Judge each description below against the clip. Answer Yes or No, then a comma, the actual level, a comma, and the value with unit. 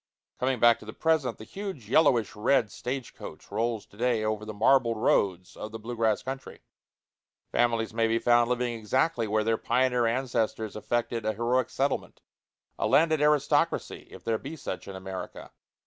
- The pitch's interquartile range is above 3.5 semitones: No, average, 3.0 semitones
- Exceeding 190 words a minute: No, average, 175 wpm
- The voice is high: No, low, 115 Hz